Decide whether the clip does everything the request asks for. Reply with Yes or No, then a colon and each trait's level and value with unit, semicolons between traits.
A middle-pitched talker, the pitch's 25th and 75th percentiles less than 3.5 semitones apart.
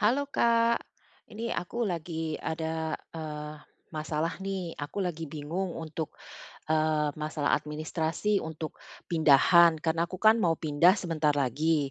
Yes: medium, 160 Hz; narrow, 2.4 semitones